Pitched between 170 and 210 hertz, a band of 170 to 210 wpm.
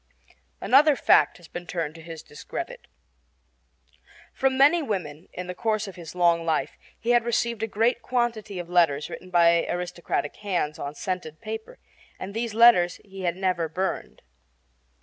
No: medium, 185 Hz; average, 160 wpm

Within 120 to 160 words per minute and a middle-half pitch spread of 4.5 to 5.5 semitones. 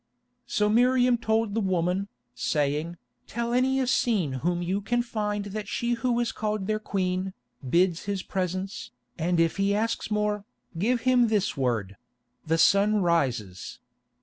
Yes: average, 145 wpm; average, 4.8 semitones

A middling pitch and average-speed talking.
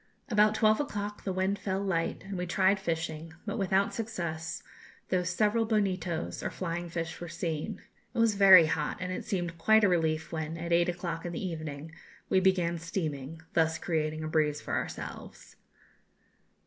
Yes: medium, 175 Hz; average, 175 wpm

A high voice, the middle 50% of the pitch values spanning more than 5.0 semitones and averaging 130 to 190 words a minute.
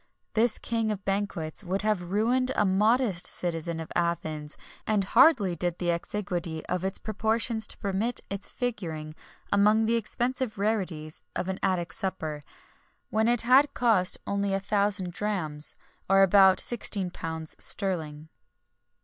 No: high, 195 Hz; average, 3.9 semitones; slow, 135 wpm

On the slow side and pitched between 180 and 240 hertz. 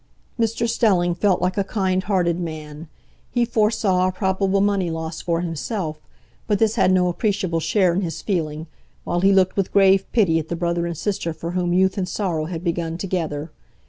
No: average, 190 wpm; medium, 185 Hz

